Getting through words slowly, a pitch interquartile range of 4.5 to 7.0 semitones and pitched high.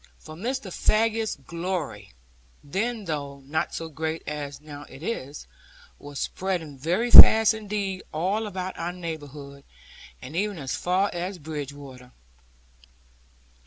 No: slow, 125 wpm; average, 5.2 semitones; medium, 165 Hz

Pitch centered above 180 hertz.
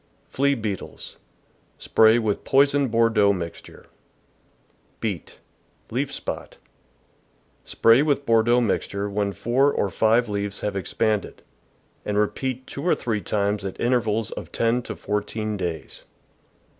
No: low, 110 Hz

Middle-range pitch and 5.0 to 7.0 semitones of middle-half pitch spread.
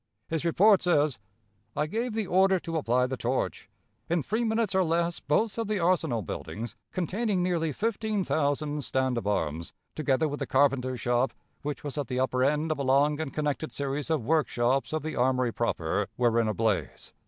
Yes: medium, 150 Hz; average, 5.3 semitones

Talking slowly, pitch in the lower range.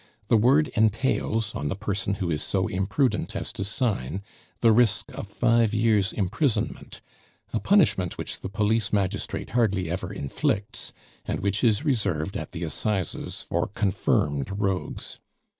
No: average, 145 wpm; low, 105 Hz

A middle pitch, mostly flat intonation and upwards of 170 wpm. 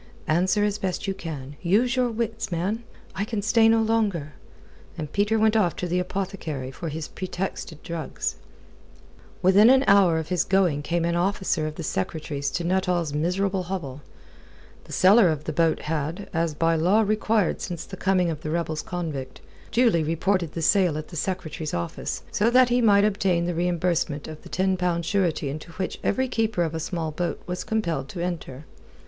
No: medium, 175 Hz; average, 4.0 semitones; average, 185 wpm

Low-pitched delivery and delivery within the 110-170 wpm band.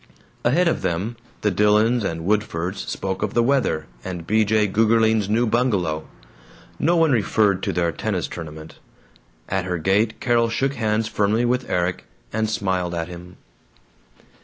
Yes: low, 105 Hz; average, 155 wpm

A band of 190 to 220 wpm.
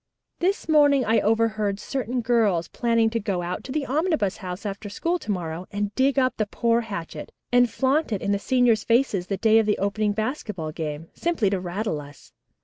Yes: average, 200 wpm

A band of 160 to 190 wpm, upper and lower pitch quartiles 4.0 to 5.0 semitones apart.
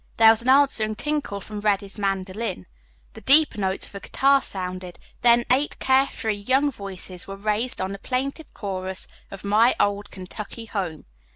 Yes: average, 170 wpm; average, 4.5 semitones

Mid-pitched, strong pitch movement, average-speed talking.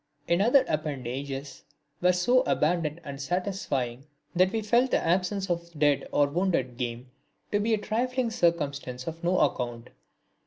Yes: medium, 170 Hz; wide, 5.9 semitones; average, 150 wpm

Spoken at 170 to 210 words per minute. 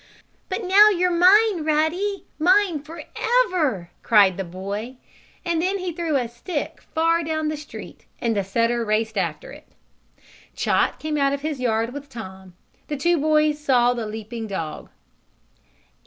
No: average, 155 wpm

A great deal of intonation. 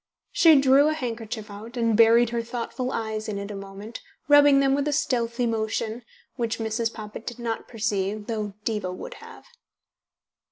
No: narrow, 2.5 semitones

